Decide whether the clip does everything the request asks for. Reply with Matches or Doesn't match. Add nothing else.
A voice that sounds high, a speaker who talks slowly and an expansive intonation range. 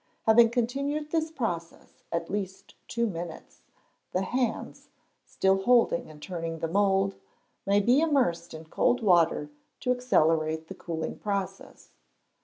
Matches